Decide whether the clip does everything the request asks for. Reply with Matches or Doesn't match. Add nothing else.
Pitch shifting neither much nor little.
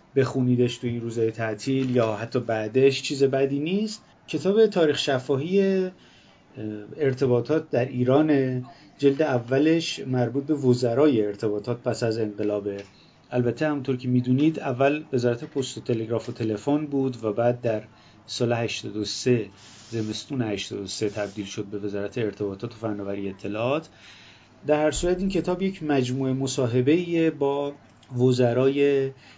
Matches